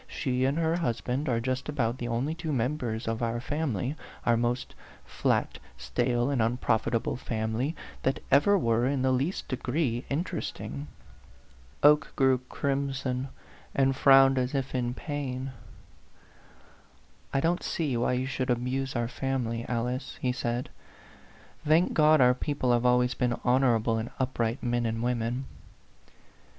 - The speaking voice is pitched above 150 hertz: No, low, 125 Hz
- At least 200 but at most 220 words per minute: No, average, 145 wpm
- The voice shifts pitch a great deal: No, narrow, 2.6 semitones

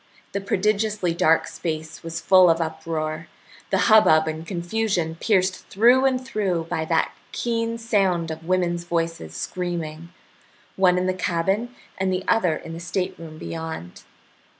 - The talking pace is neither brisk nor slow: Yes, average, 145 wpm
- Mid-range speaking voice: Yes, medium, 175 Hz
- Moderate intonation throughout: Yes, average, 3.5 semitones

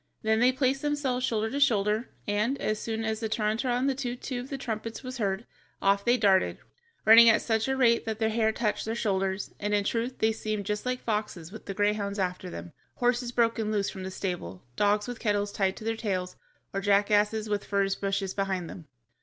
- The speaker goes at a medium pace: No, fast, 215 wpm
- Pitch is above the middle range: Yes, high, 215 Hz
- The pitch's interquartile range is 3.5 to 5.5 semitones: No, average, 2.9 semitones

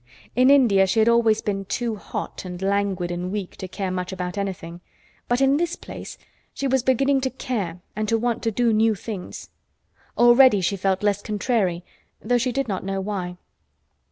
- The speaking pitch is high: Yes, high, 210 Hz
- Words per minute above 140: Yes, average, 185 wpm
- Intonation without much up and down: No, average, 4.2 semitones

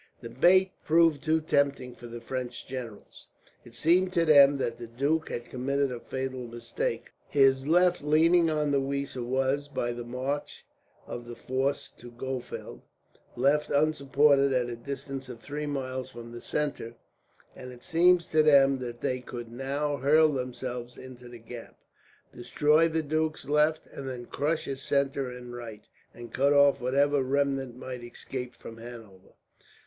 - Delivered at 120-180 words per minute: Yes, average, 165 wpm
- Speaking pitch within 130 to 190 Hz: Yes, low, 135 Hz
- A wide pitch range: No, average, 3.2 semitones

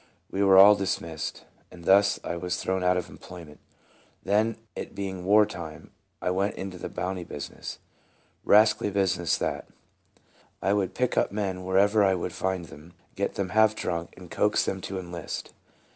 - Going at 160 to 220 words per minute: Yes, average, 170 wpm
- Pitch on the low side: Yes, very low, 95 Hz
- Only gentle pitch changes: Yes, narrow, 2.0 semitones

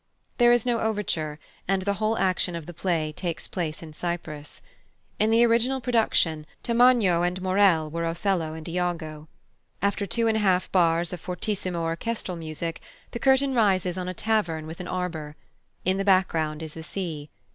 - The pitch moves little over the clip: No, average, 4.3 semitones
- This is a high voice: No, medium, 180 Hz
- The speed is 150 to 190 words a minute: Yes, average, 175 wpm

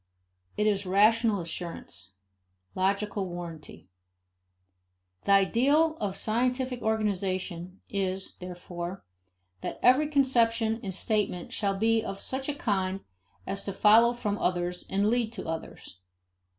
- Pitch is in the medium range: No, high, 200 Hz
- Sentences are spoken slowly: Yes, slow, 125 wpm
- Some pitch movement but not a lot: Yes, average, 3.6 semitones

